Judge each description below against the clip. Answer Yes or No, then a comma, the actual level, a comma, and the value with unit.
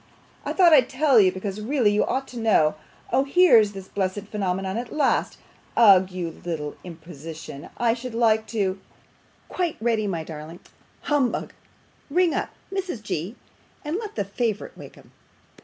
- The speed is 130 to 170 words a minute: Yes, average, 155 wpm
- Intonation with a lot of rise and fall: Yes, wide, 5.7 semitones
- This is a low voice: No, high, 215 Hz